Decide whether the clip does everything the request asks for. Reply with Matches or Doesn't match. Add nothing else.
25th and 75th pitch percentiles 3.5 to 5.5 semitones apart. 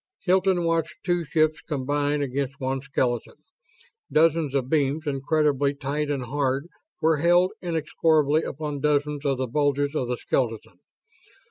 Doesn't match